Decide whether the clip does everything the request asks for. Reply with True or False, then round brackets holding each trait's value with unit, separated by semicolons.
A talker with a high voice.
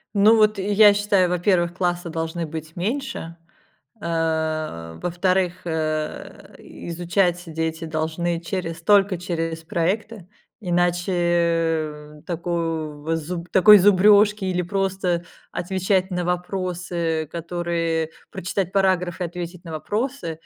False (175 Hz)